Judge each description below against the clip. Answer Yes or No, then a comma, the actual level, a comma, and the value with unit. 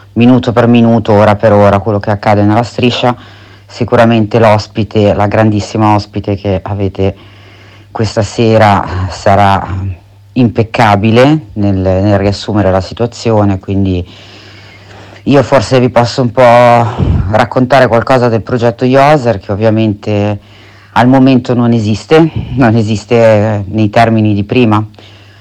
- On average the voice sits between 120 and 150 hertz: No, low, 105 Hz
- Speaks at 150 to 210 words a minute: No, average, 120 wpm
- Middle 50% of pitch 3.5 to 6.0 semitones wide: No, average, 2.9 semitones